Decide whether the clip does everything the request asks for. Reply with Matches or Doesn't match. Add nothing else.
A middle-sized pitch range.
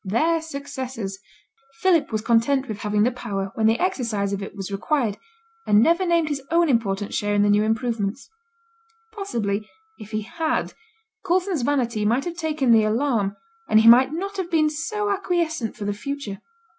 Doesn't match